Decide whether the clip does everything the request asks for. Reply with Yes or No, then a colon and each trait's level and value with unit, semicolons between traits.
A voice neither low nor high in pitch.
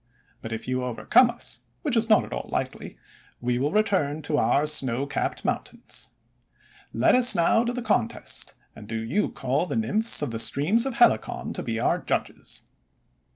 Yes: medium, 150 Hz